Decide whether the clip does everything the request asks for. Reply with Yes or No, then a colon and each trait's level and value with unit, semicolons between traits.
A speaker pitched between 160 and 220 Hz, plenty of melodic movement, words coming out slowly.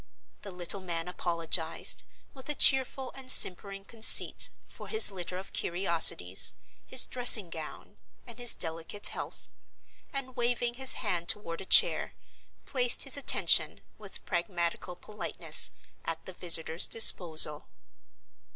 Yes: high, 190 Hz; wide, 6.3 semitones; slow, 125 wpm